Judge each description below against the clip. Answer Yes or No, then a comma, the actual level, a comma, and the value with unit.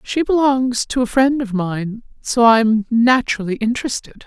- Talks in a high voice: Yes, high, 235 Hz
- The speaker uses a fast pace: No, average, 170 wpm